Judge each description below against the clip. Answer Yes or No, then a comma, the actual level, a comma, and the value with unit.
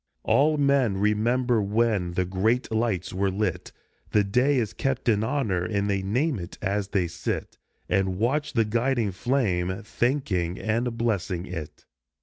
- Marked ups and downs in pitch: No, average, 4.3 semitones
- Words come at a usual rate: Yes, average, 150 wpm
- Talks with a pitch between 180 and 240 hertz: No, low, 105 Hz